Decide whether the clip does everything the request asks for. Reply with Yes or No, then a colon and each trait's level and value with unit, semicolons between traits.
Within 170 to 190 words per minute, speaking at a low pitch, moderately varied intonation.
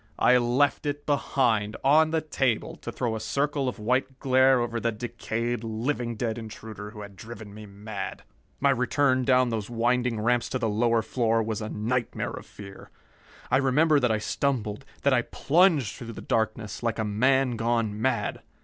Yes: average, 180 wpm; low, 120 Hz; average, 3.1 semitones